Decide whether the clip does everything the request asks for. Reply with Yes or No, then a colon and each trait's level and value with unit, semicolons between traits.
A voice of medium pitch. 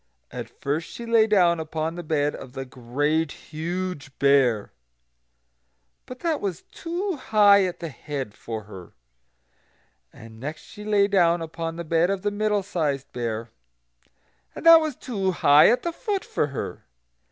Yes: medium, 165 Hz